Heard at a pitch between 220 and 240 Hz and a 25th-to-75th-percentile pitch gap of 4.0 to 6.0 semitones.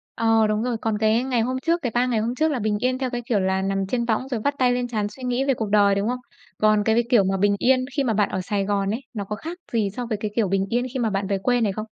No: high, 225 Hz; average, 3.3 semitones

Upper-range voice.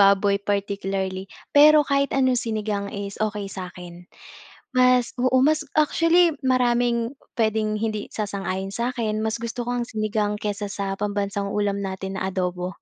Yes: high, 210 Hz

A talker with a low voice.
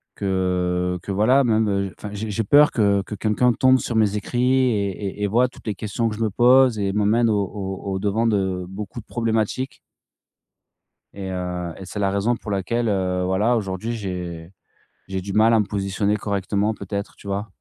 Yes: low, 100 Hz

